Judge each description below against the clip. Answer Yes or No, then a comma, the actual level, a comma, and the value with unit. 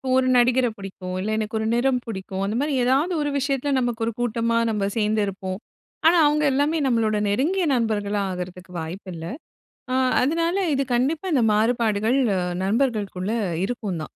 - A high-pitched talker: Yes, high, 230 Hz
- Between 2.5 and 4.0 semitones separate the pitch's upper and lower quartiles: No, average, 4.7 semitones